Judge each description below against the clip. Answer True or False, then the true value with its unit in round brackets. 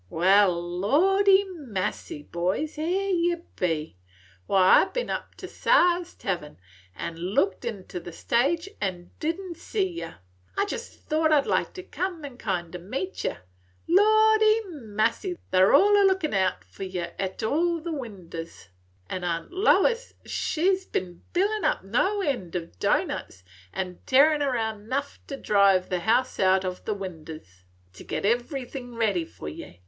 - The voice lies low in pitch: False (230 Hz)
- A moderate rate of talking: True (165 wpm)